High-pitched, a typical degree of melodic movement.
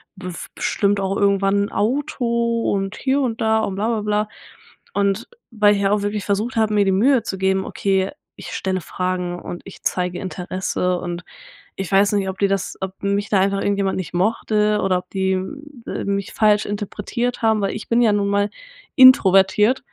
No: high, 200 Hz; narrow, 1.9 semitones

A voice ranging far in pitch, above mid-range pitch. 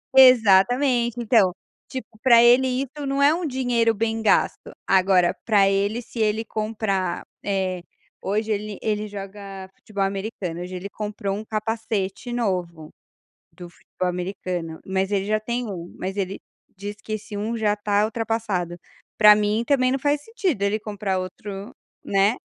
No: average, 3.2 semitones; high, 210 Hz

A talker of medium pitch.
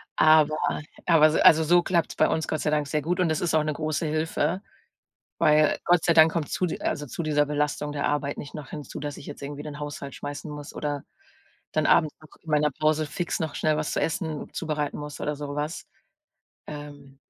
Yes: medium, 150 Hz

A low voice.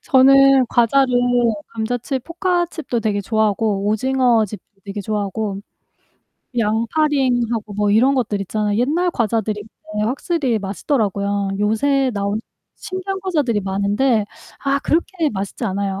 No: high, 225 Hz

